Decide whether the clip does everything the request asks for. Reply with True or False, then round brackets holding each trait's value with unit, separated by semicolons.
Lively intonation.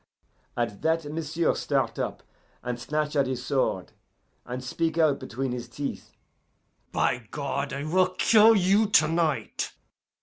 False (4.4 semitones)